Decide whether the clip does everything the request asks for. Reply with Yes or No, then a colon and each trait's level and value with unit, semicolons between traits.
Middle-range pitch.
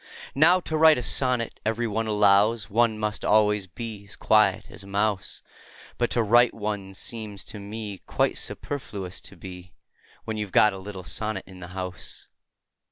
No: low, 105 Hz